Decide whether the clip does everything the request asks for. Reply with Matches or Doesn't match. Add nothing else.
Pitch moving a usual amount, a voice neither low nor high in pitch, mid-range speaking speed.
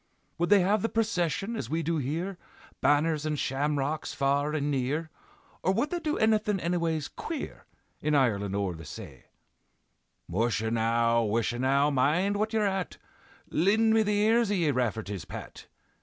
Doesn't match